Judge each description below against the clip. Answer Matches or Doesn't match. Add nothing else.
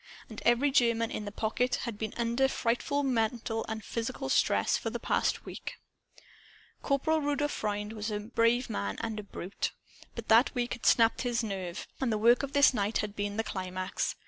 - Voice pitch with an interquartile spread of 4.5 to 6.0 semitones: Doesn't match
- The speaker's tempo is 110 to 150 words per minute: Doesn't match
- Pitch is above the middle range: Matches